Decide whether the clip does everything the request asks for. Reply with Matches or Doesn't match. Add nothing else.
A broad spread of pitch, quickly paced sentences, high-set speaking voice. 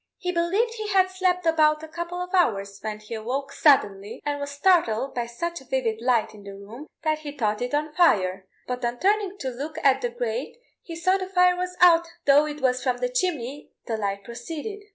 Matches